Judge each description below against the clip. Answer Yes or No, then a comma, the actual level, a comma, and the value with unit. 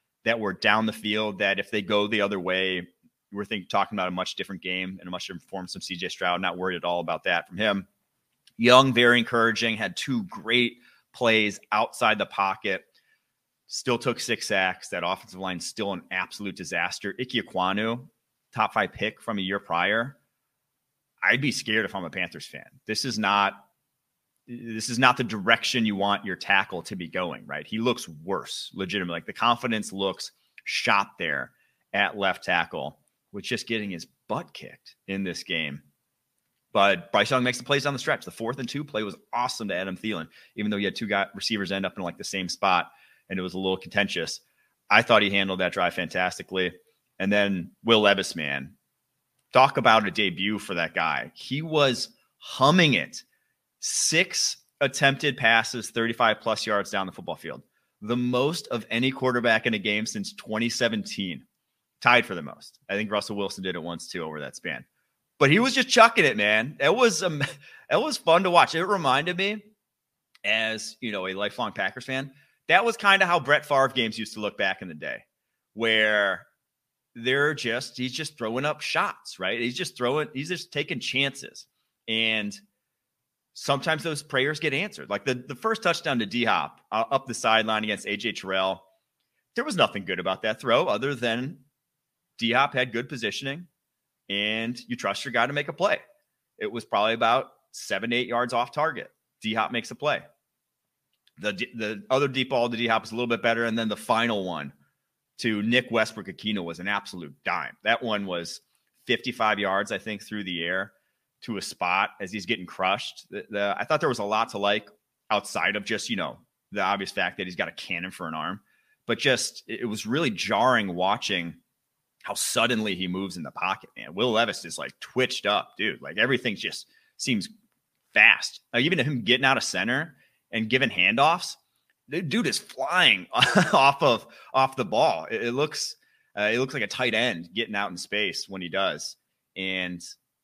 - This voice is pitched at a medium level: No, low, 115 Hz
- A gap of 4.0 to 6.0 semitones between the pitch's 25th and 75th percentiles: Yes, average, 4.6 semitones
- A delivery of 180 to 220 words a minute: Yes, average, 195 wpm